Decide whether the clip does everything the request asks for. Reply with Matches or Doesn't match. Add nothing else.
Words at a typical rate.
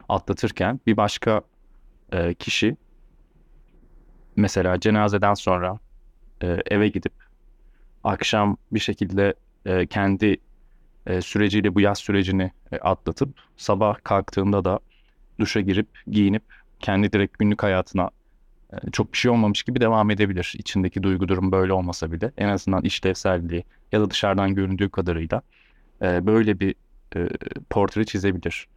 Matches